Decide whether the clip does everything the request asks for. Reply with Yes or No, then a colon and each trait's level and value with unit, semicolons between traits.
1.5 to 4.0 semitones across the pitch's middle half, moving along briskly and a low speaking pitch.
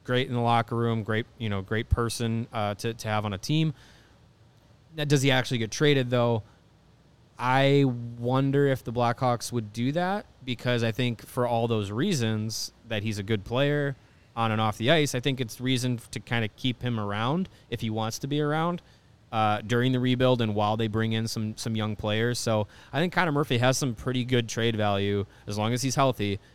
Yes: average, 3.0 semitones; fast, 215 wpm; low, 120 Hz